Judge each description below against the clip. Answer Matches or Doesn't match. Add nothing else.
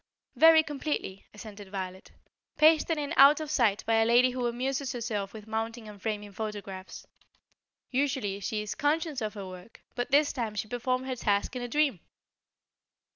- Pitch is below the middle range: Doesn't match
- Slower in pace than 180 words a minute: Matches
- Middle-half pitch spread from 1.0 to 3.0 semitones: Doesn't match